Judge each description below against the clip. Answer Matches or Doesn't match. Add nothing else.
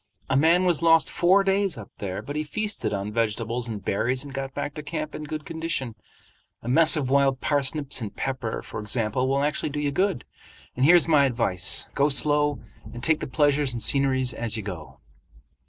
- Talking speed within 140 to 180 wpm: Doesn't match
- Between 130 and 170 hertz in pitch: Matches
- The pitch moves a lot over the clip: Doesn't match